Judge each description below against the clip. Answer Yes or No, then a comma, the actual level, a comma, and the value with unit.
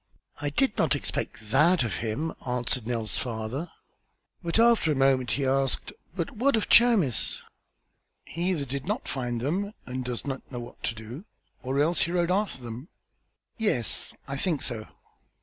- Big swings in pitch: Yes, wide, 6.0 semitones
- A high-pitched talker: No, low, 135 Hz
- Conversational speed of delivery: Yes, average, 165 wpm